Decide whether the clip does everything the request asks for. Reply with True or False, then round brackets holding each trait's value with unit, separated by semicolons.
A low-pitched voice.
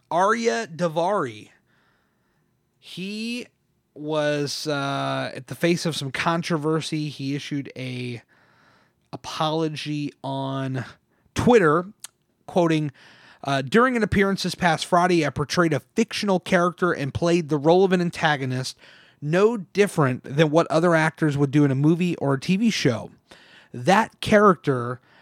False (160 Hz)